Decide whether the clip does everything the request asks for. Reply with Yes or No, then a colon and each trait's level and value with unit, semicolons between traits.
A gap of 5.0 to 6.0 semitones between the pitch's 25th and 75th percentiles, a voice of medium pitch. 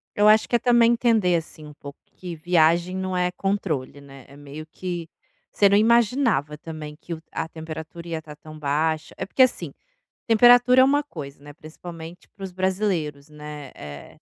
Yes: average, 5.3 semitones; medium, 170 Hz